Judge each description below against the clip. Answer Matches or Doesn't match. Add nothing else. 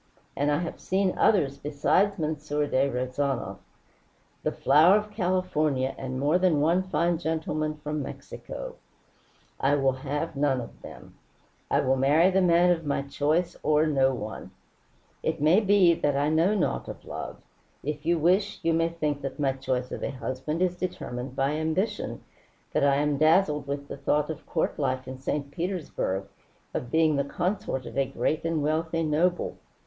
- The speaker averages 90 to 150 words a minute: Doesn't match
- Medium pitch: Matches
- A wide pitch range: Doesn't match